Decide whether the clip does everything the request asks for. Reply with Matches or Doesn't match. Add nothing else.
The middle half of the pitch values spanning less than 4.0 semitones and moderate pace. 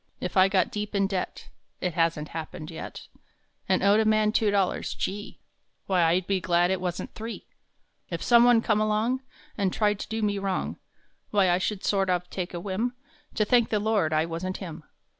Doesn't match